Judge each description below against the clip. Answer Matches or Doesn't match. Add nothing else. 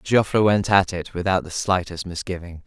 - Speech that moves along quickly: Doesn't match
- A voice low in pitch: Matches